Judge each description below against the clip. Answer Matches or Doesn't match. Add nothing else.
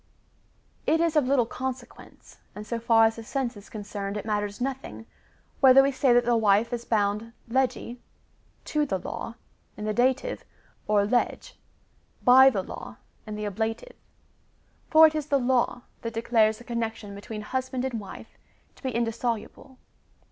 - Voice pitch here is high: Matches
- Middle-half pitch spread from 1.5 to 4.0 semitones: Matches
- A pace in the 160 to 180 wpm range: Matches